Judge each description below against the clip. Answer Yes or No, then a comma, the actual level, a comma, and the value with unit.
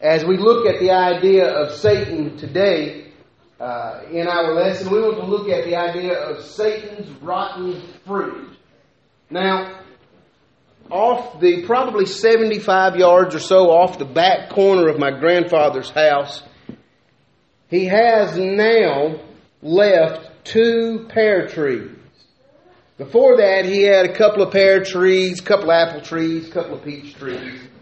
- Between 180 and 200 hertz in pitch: Yes, medium, 185 Hz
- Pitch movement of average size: Yes, average, 3.6 semitones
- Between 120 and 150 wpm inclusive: Yes, average, 140 wpm